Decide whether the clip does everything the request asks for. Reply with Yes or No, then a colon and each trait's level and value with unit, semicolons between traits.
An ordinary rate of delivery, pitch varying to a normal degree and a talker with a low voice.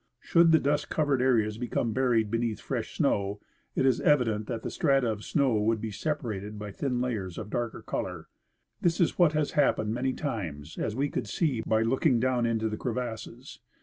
Yes: average, 195 wpm; average, 4.0 semitones; low, 120 Hz